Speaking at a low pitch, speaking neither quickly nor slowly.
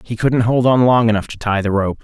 No: low, 115 Hz; fast, 295 wpm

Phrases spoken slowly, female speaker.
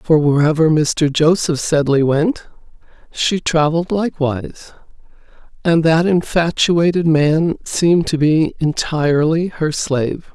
Yes: slow, 110 wpm; female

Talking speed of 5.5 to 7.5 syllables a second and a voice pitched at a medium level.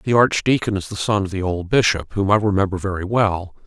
No: 5.7 syllables/s; low, 100 Hz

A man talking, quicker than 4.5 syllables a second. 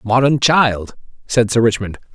No: male; 4.3 syllables/s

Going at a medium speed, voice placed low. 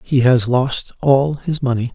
Yes: average, 185 wpm; low, 130 Hz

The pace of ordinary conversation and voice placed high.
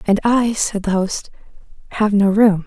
Yes: average, 180 wpm; high, 210 Hz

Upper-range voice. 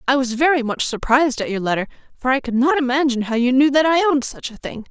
Yes: very high, 260 Hz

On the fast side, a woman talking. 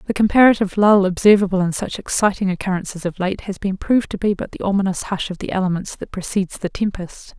Yes: fast, 210 wpm; female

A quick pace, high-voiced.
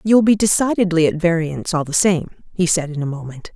No: fast, 220 wpm; medium, 170 Hz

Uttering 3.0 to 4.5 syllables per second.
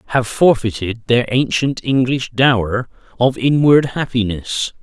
Yes: 4.1 syllables/s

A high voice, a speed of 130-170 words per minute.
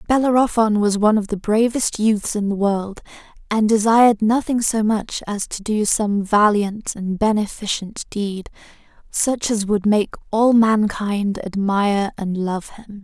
Yes: high, 210 Hz; average, 150 wpm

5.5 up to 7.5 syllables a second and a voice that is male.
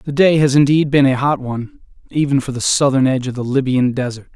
Yes: 6.0 syllables/s; male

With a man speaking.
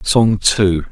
Yes: male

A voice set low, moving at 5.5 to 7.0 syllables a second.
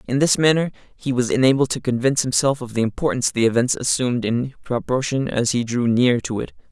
Yes: low, 125 Hz; 6.0 syllables/s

